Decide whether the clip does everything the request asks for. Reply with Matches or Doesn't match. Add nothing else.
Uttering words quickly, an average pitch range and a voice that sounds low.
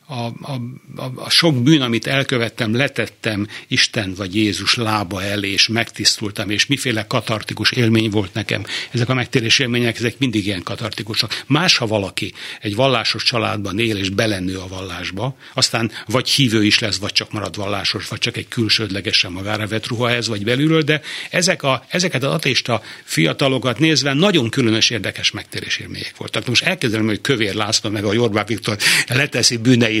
Matches